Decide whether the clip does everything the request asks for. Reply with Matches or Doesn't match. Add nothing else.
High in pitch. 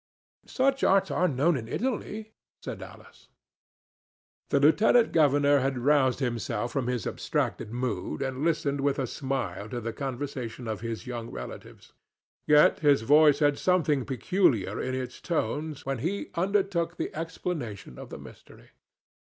Doesn't match